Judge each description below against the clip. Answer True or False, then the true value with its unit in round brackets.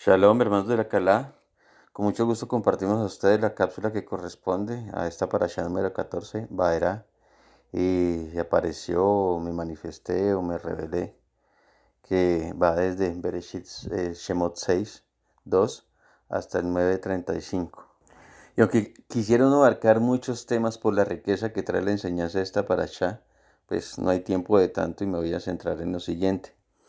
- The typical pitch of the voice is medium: False (95 Hz)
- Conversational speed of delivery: True (155 wpm)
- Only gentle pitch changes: False (3.6 semitones)